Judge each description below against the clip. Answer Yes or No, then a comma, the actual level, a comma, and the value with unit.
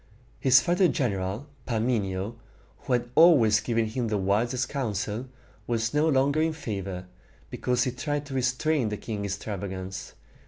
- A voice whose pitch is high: No, low, 120 Hz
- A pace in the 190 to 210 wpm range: No, average, 145 wpm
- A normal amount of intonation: Yes, average, 4.7 semitones